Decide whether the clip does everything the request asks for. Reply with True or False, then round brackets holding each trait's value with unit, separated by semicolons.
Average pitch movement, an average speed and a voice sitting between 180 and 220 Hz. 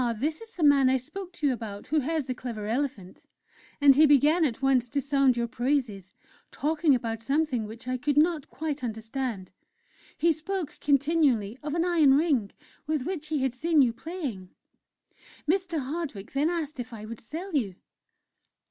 False (4.7 semitones; 175 wpm; 275 Hz)